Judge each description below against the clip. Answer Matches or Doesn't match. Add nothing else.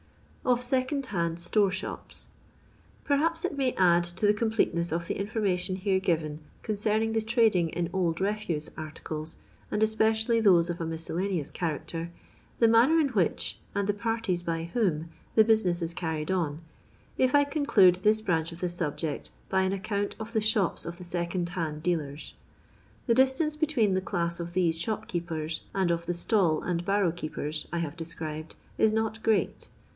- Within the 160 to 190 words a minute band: Matches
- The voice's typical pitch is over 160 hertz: Matches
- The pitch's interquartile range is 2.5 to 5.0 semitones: Matches